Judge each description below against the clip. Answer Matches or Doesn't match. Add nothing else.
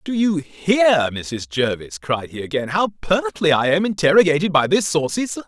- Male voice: Matches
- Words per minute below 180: Doesn't match